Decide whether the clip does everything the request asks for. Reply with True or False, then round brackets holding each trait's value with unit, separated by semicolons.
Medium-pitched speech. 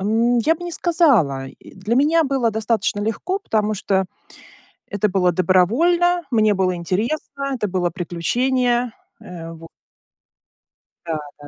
False (215 Hz)